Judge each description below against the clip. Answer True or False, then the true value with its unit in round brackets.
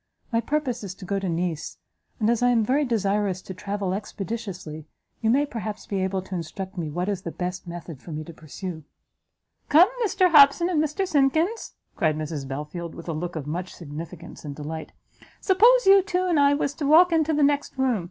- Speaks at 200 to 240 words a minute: True (205 wpm)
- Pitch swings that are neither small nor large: False (9.0 semitones)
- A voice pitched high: True (200 Hz)